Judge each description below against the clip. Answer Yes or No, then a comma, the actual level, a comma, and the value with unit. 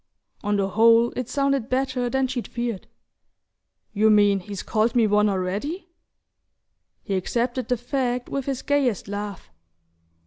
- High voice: Yes, high, 235 Hz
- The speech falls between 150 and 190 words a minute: No, average, 140 wpm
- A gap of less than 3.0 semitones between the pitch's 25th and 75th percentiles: No, average, 3.8 semitones